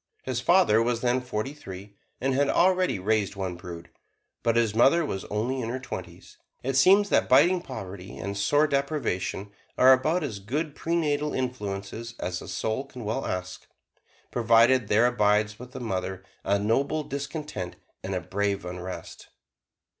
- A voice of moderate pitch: No, low, 120 Hz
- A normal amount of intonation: No, wide, 5.7 semitones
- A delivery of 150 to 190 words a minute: Yes, average, 160 wpm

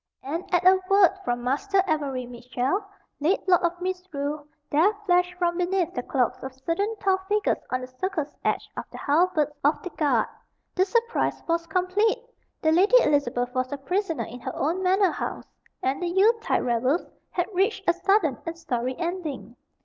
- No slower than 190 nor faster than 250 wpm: No, average, 175 wpm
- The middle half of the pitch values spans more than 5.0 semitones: Yes, wide, 5.5 semitones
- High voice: Yes, very high, 335 Hz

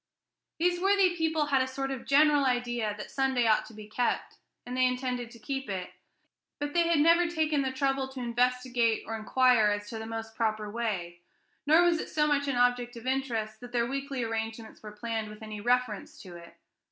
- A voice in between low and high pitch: No, high, 245 Hz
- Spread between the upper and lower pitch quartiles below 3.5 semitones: No, average, 3.8 semitones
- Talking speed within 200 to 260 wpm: Yes, fast, 205 wpm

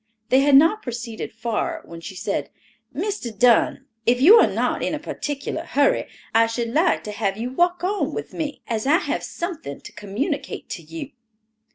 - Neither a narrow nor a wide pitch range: No, wide, 5.9 semitones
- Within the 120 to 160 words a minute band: No, average, 185 wpm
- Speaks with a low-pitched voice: No, very high, 250 Hz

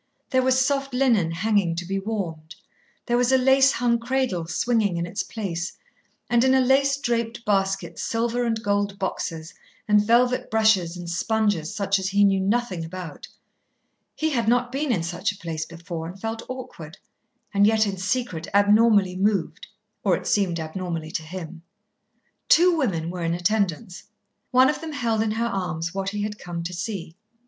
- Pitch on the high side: Yes, high, 205 Hz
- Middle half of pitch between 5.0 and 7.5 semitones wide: Yes, average, 5.3 semitones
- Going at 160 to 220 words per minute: Yes, average, 175 wpm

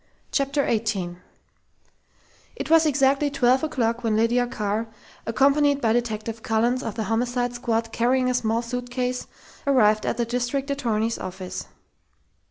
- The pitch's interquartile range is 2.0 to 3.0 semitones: Yes, average, 2.7 semitones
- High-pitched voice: Yes, high, 240 Hz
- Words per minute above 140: No, slow, 135 wpm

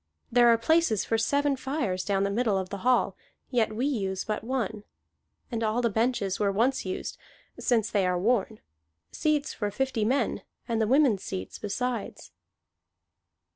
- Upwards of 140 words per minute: Yes, average, 165 wpm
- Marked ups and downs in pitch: No, average, 4.0 semitones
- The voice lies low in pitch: No, high, 225 Hz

